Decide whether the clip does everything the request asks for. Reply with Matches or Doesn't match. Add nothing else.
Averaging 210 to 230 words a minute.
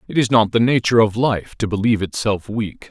Matches